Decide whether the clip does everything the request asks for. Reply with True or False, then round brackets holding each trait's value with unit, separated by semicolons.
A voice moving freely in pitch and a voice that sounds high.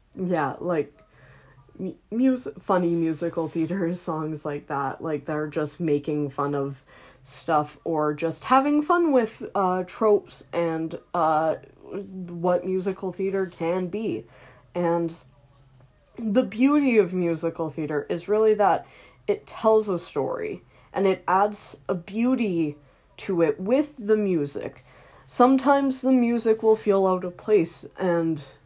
False (5.8 semitones; 175 Hz)